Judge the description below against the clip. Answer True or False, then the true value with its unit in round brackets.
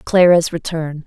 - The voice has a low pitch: False (165 Hz)